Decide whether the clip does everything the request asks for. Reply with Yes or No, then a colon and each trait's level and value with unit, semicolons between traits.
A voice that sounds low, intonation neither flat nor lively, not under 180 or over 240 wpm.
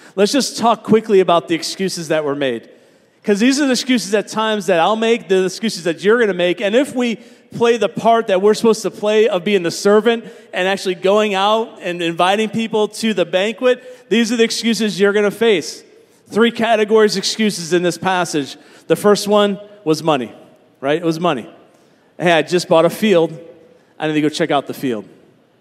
No: high, 205 Hz; average, 4.6 semitones; fast, 205 wpm